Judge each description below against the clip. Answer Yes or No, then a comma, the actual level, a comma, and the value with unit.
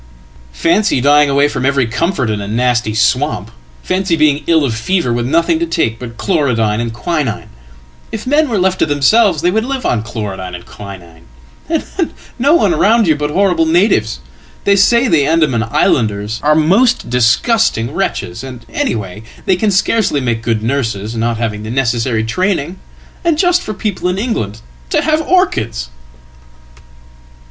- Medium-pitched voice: Yes, medium, 145 Hz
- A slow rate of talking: No, average, 155 wpm